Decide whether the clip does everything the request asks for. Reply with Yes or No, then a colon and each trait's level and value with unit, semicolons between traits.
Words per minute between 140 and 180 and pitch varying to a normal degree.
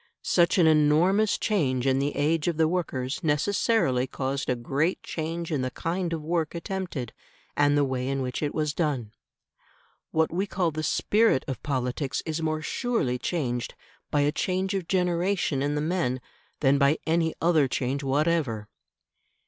Yes: average, 165 wpm; average, 4.1 semitones